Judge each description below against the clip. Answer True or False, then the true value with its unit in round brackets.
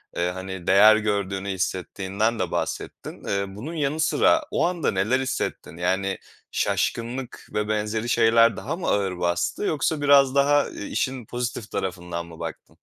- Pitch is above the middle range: False (110 Hz)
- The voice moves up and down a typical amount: False (5.8 semitones)